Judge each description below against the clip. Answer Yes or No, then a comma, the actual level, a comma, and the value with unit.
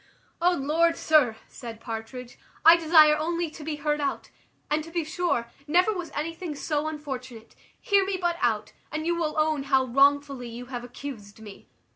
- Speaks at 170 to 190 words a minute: Yes, average, 175 wpm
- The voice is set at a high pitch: Yes, very high, 300 Hz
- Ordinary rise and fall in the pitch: Yes, average, 4.8 semitones